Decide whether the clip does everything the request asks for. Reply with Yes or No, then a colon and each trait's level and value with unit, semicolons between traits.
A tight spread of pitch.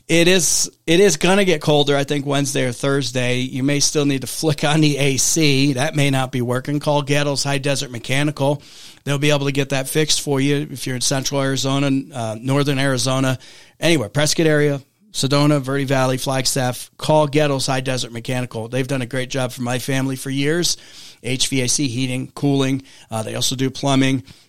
Yes: narrow, 2.0 semitones